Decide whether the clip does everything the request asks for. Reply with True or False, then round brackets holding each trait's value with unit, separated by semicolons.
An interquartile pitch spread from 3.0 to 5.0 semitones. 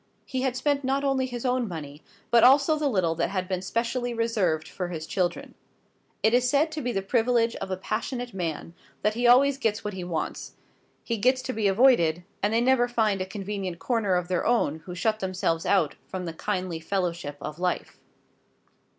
False (5.4 semitones)